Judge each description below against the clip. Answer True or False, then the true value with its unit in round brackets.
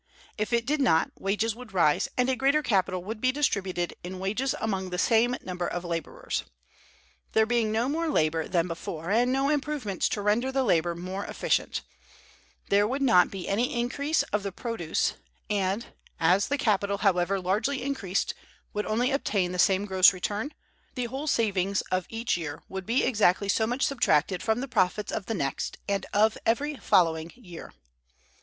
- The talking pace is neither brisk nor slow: True (175 wpm)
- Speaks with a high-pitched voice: True (205 Hz)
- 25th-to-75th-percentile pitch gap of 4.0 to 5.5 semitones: True (4.9 semitones)